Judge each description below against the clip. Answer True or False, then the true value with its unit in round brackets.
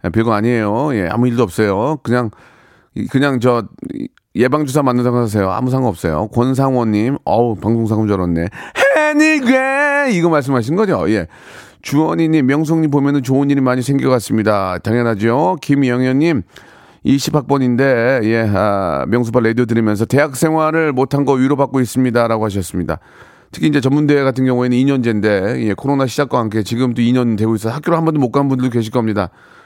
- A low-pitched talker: True (125 Hz)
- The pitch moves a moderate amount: True (4.1 semitones)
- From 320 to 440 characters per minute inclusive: True (370 characters per minute)